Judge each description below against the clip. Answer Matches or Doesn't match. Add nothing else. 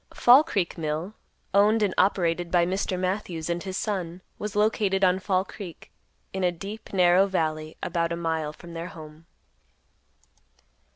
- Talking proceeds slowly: Doesn't match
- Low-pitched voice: Doesn't match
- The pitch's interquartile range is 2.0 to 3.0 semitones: Matches